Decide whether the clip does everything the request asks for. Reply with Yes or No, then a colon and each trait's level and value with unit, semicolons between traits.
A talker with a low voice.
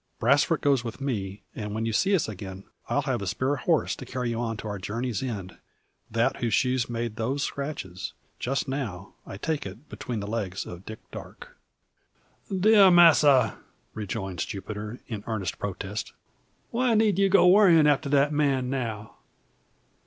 Yes: low, 120 Hz